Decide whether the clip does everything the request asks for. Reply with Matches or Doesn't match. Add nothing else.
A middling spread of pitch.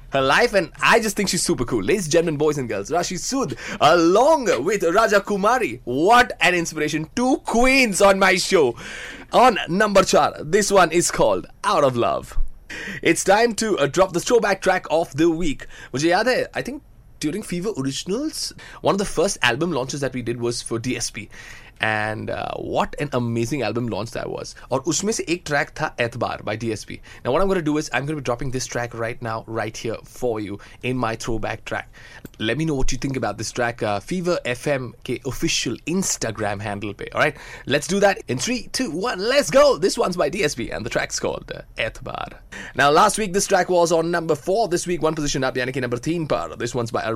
Doesn't match